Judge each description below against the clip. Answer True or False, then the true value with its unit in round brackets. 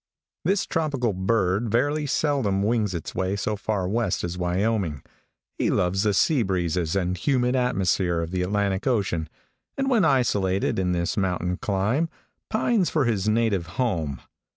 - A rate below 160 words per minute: True (150 wpm)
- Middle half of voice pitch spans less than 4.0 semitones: False (5.3 semitones)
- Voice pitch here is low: True (100 Hz)